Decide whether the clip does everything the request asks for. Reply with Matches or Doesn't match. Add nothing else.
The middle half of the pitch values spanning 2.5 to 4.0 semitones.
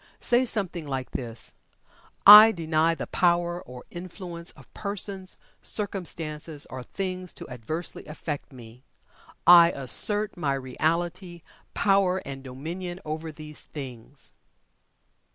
Doesn't match